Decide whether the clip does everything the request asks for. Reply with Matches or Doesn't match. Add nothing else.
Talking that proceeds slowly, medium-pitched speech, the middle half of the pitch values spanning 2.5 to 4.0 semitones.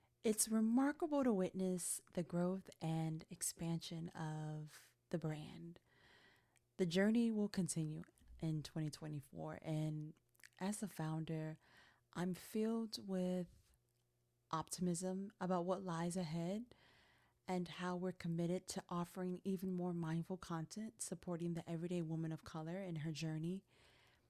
Matches